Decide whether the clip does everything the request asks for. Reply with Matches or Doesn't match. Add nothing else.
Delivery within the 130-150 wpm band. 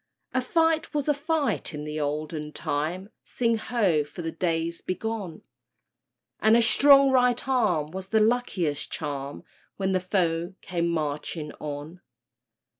Matches